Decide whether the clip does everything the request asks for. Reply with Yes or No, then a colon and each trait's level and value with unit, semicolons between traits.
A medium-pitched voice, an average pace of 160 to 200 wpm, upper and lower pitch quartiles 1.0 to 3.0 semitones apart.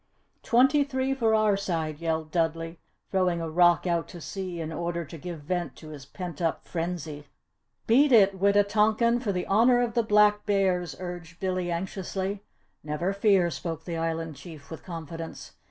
No: medium, 180 Hz; average, 170 wpm; average, 3.8 semitones